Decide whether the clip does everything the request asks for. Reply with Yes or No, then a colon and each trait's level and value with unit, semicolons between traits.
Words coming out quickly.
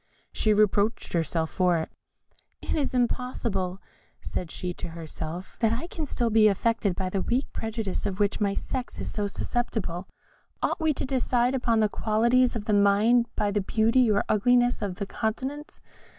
No: average, 175 wpm